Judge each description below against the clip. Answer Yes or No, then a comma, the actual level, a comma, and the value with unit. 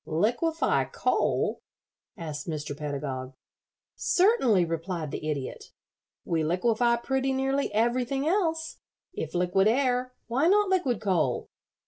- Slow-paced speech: Yes, slow, 110 wpm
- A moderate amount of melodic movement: No, wide, 8.8 semitones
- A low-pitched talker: No, high, 230 Hz